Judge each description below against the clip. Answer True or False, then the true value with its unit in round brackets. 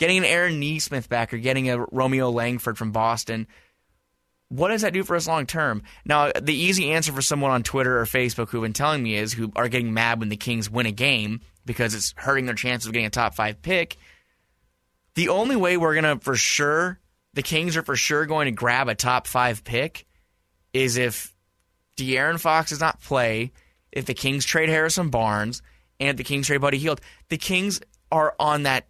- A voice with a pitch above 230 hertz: False (130 Hz)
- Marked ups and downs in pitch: False (4.9 semitones)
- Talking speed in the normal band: False (210 wpm)